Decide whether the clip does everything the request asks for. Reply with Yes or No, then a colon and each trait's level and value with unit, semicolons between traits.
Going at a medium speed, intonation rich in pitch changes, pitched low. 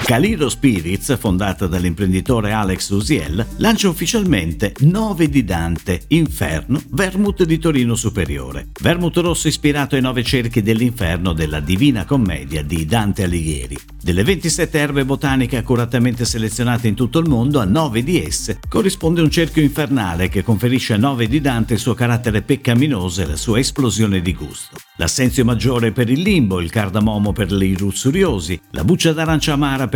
Yes: average, 155 wpm; wide, 6.9 semitones; low, 120 Hz